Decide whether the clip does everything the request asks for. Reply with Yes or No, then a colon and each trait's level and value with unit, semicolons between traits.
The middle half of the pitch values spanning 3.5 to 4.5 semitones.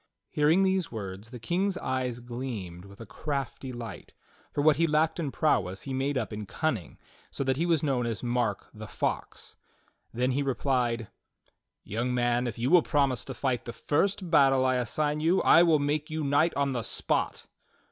Yes: average, 4.2 semitones